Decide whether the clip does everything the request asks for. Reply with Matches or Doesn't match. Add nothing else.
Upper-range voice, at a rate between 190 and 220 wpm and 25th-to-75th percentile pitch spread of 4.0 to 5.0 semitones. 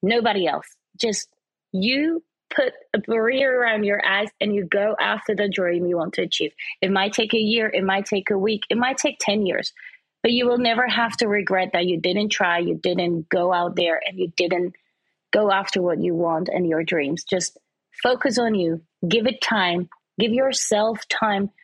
Matches